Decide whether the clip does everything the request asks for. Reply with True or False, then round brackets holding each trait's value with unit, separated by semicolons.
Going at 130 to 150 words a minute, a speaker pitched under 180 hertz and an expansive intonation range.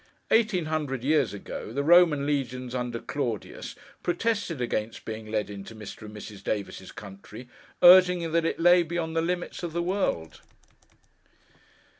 True (145 wpm; 140 Hz; 7.8 semitones)